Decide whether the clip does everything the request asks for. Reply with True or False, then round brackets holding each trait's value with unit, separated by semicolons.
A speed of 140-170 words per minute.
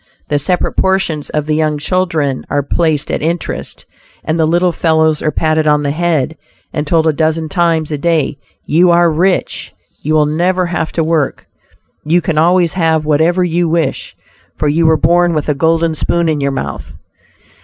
False (185 wpm)